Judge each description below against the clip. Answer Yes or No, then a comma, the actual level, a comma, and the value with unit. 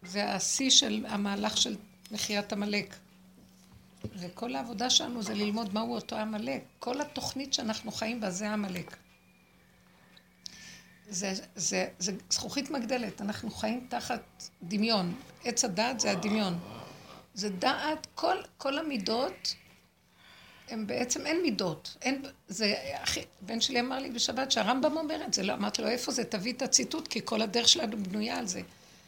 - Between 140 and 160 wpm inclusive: Yes, average, 145 wpm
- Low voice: No, high, 220 Hz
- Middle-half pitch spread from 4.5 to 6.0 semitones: No, average, 3.8 semitones